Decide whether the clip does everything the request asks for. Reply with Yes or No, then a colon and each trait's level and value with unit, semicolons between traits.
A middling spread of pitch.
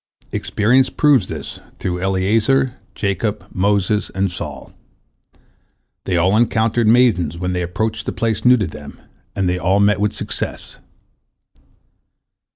Yes: average, 3.6 semitones